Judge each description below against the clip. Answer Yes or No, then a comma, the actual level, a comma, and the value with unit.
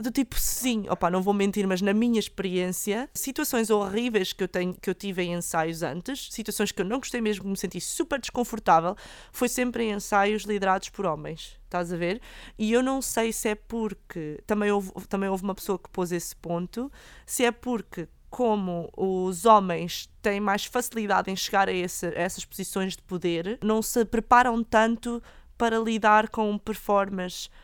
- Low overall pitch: No, high, 205 Hz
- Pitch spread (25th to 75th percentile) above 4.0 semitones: No, average, 3.6 semitones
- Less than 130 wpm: No, fast, 185 wpm